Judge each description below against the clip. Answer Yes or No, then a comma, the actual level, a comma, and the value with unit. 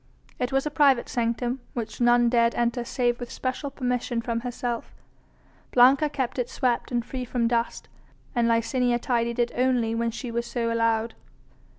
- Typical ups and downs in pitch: No, narrow, 1.3 semitones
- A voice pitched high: Yes, high, 240 Hz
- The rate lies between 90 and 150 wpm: No, average, 170 wpm